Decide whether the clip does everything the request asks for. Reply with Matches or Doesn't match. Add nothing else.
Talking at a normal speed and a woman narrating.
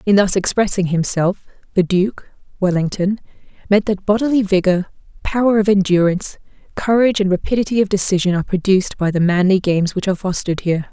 Matches